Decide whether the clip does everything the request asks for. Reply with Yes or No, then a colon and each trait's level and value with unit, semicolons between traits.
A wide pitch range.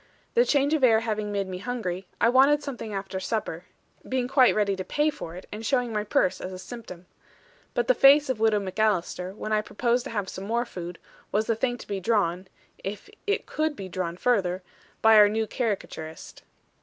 No: average, 4.7 semitones